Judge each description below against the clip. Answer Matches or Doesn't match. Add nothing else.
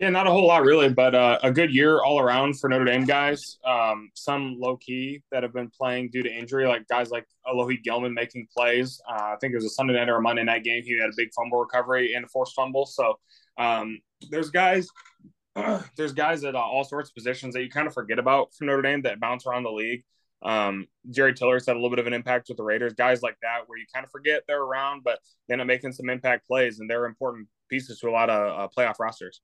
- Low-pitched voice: Matches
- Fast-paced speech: Matches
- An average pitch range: Doesn't match